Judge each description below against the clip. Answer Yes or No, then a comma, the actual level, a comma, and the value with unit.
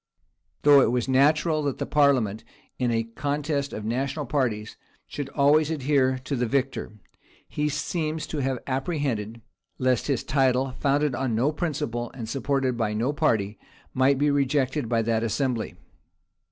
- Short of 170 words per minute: Yes, average, 155 wpm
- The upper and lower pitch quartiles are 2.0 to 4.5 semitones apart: Yes, average, 3.5 semitones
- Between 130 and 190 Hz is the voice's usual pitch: Yes, low, 135 Hz